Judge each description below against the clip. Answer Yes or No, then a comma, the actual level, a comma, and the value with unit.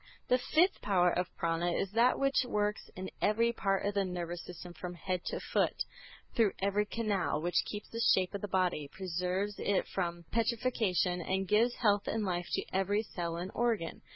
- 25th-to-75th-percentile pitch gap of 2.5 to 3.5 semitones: Yes, average, 3.2 semitones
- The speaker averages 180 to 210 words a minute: Yes, average, 185 wpm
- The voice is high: Yes, high, 195 Hz